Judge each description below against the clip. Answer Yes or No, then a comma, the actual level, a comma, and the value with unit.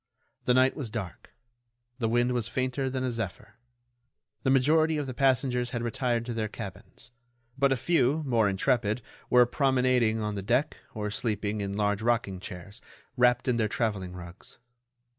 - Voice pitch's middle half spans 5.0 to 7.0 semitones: No, average, 3.3 semitones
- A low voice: Yes, low, 120 Hz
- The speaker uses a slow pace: No, average, 165 wpm